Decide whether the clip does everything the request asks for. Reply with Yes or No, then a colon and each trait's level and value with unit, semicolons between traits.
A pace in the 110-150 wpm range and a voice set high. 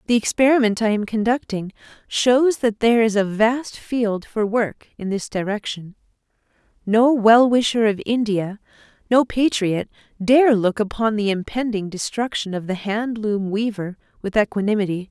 Yes: average, 145 wpm; high, 215 Hz